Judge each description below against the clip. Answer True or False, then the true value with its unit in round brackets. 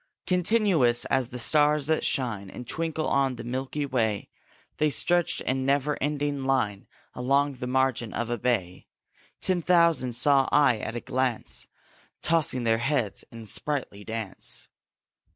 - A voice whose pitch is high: False (130 Hz)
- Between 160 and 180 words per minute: False (145 wpm)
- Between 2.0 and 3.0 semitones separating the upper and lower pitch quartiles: False (3.8 semitones)